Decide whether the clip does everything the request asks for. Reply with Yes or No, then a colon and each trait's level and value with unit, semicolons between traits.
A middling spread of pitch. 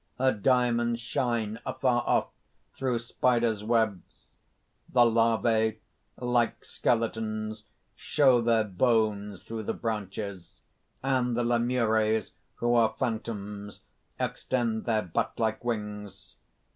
No: narrow, 2.0 semitones